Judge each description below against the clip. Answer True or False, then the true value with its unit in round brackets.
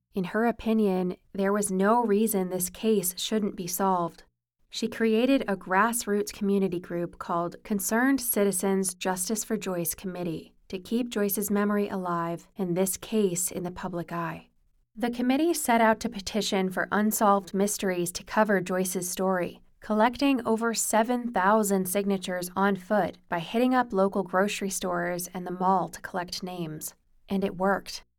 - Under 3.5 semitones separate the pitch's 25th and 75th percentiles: True (3.1 semitones)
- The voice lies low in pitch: False (195 Hz)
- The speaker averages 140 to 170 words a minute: True (150 wpm)